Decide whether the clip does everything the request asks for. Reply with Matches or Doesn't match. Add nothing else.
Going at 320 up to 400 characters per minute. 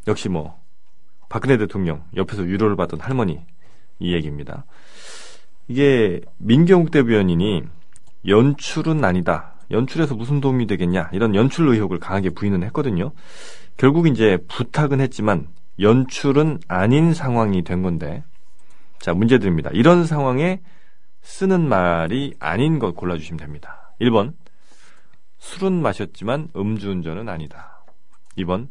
Doesn't match